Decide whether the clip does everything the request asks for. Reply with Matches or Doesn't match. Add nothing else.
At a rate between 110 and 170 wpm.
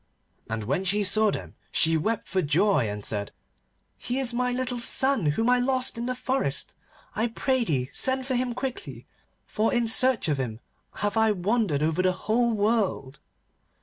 Doesn't match